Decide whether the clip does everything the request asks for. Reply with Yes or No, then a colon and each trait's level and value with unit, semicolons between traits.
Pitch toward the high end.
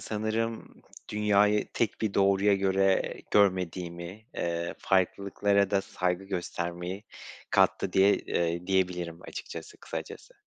No: very low, 95 Hz